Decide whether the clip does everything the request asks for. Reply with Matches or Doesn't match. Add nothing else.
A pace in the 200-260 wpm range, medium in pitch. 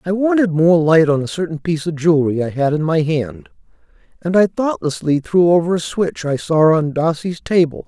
Matches